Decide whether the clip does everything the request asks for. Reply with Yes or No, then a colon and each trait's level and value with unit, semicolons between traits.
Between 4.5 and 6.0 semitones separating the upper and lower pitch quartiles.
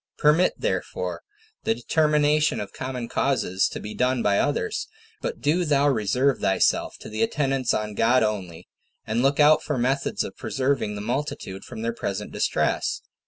Yes: average, 5.3 semitones